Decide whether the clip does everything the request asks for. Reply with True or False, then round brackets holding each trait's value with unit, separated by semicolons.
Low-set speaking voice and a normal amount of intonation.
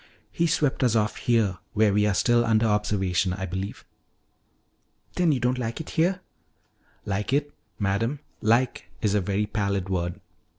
True (105 Hz; 4.0 semitones)